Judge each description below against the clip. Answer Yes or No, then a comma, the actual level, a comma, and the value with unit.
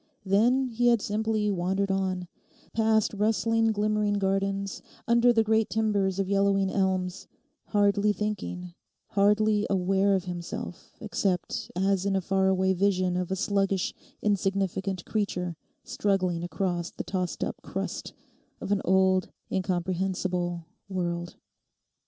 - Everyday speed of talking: No, slow, 125 wpm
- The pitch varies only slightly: Yes, narrow, 2.1 semitones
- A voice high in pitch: Yes, high, 195 Hz